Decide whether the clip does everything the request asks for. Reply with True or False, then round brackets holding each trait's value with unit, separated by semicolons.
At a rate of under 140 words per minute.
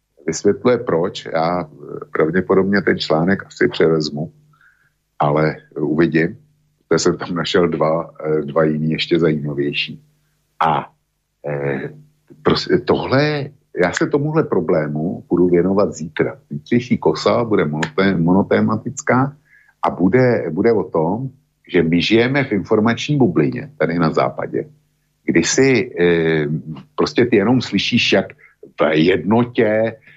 True (115 wpm)